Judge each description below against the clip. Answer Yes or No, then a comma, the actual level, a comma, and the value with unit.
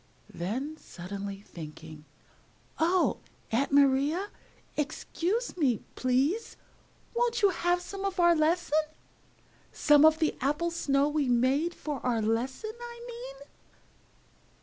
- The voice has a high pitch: Yes, very high, 300 Hz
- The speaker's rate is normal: No, slow, 115 wpm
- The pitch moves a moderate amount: No, wide, 5.9 semitones